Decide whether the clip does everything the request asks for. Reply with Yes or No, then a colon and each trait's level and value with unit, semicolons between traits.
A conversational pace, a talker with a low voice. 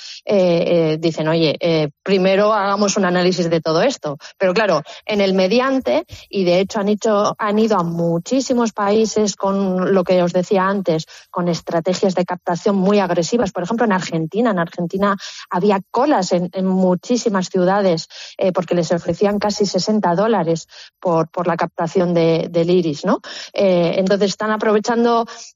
No: average, 165 wpm; high, 190 Hz